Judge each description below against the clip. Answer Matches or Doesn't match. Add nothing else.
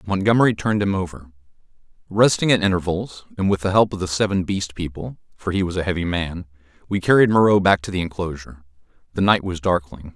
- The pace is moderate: Matches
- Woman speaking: Doesn't match